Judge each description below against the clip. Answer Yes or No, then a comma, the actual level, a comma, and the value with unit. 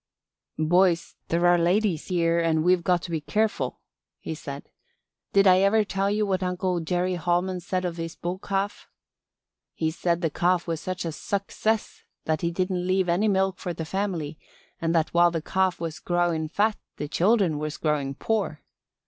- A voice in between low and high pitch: Yes, medium, 175 Hz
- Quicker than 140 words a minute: Yes, average, 180 wpm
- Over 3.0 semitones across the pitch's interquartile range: No, narrow, 2.4 semitones